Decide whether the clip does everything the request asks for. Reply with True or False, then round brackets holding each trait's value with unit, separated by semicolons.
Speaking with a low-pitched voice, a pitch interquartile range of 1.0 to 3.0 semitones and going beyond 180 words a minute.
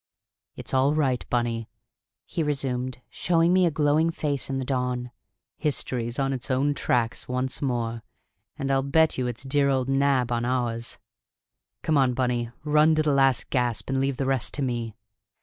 False (130 Hz; 2.6 semitones; 175 wpm)